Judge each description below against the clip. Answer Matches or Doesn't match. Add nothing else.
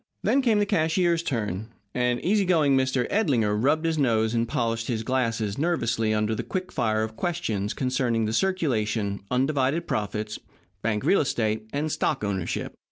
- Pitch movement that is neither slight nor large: Doesn't match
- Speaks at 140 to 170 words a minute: Matches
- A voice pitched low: Matches